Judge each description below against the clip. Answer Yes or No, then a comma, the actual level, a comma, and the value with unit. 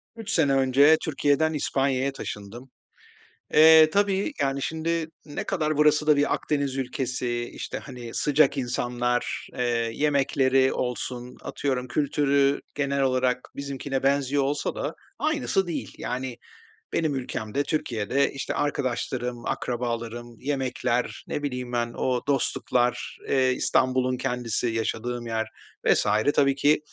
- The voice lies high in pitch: No, low, 135 Hz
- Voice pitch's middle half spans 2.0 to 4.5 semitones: Yes, average, 2.9 semitones